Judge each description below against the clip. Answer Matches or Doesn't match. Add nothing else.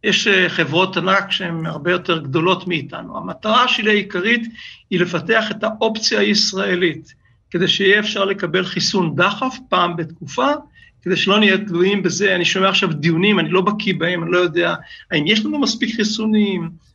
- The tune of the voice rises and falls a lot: Doesn't match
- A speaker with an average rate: Doesn't match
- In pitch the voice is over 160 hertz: Matches